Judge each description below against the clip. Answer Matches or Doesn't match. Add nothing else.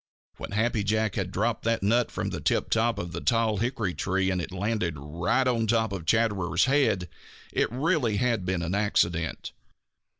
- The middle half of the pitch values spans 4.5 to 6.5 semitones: Doesn't match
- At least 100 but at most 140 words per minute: Doesn't match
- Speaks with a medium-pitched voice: Doesn't match